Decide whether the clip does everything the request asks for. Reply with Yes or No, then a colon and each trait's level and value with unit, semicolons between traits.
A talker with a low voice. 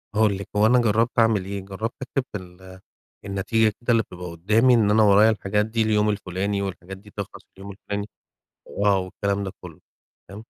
Yes: low, 100 Hz